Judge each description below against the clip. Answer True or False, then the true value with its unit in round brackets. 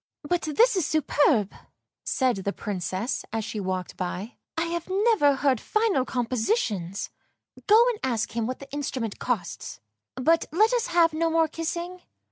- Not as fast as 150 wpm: False (170 wpm)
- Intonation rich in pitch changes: True (7.4 semitones)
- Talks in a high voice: True (280 Hz)